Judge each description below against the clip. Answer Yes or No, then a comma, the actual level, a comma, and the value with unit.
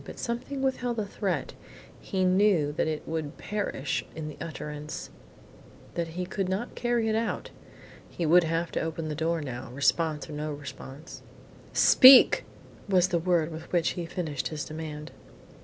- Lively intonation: No, average, 3.9 semitones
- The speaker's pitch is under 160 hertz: No, medium, 165 Hz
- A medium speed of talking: Yes, average, 165 wpm